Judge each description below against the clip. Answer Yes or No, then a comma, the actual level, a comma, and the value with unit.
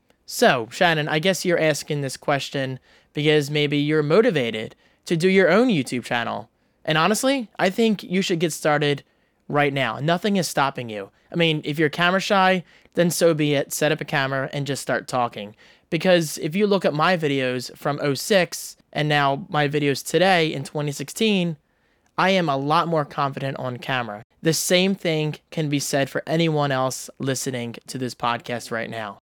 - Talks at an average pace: Yes, average, 180 wpm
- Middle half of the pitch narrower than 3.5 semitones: No, average, 4.3 semitones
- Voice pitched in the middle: Yes, medium, 150 Hz